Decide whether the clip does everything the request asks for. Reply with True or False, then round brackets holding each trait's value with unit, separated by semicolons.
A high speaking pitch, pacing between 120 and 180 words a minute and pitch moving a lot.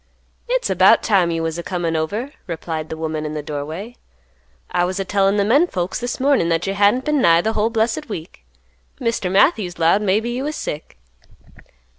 False (195 Hz; 190 wpm; 5.8 semitones)